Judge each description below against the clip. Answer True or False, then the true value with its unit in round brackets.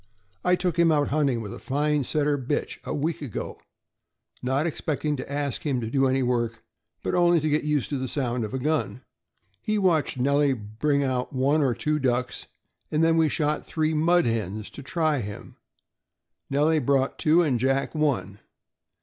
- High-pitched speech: False (140 Hz)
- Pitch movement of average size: True (3.4 semitones)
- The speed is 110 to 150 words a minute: False (185 wpm)